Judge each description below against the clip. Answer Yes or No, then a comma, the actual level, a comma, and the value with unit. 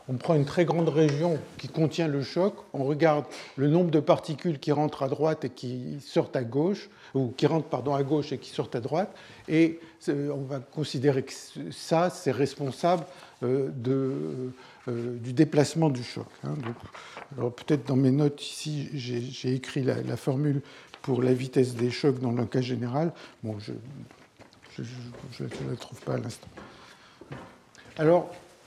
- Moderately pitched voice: Yes, medium, 145 Hz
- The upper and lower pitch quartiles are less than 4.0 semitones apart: Yes, average, 3.5 semitones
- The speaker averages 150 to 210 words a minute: Yes, average, 165 wpm